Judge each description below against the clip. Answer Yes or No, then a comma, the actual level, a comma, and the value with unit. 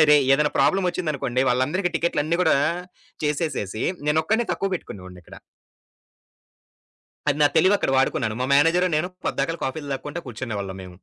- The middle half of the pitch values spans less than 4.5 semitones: No, average, 4.8 semitones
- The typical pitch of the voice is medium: Yes, medium, 150 Hz